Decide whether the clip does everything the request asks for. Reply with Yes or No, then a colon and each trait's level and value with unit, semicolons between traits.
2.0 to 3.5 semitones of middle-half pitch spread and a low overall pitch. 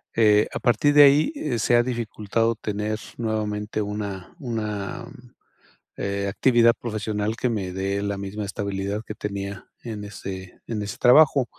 Yes: average, 2.7 semitones; low, 105 Hz